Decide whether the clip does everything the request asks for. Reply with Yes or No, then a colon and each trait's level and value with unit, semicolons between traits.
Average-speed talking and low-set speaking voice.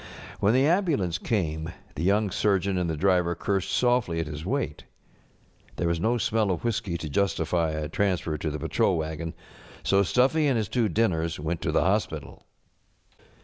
Yes: average, 180 wpm; very low, 90 Hz